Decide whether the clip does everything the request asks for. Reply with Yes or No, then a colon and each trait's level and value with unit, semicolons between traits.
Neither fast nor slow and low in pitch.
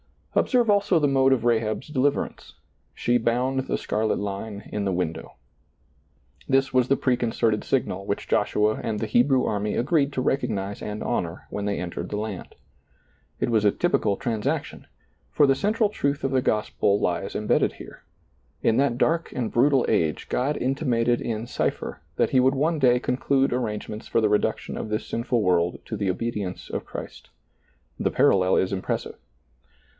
Yes: average, 170 wpm; low, 120 Hz